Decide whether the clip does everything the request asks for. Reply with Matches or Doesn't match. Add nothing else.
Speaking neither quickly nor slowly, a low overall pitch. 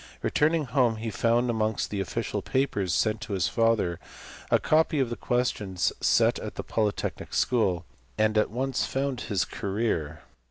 Matches